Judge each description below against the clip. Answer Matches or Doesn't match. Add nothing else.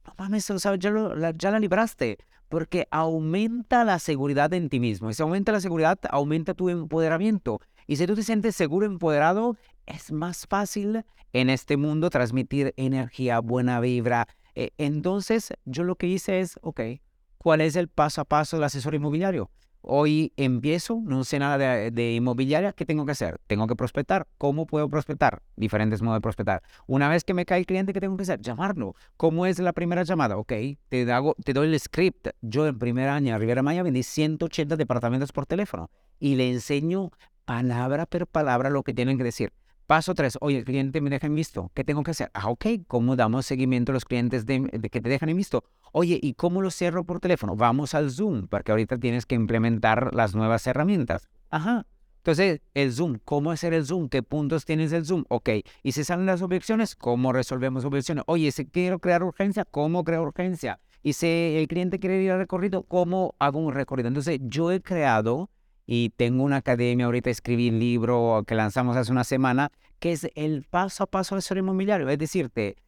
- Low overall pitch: Doesn't match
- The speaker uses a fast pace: Matches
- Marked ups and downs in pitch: Matches